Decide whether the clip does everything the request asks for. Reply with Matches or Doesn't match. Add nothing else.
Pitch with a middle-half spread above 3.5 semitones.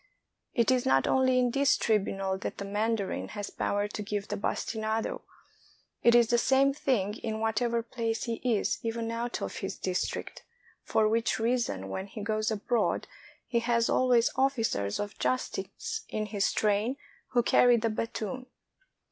Doesn't match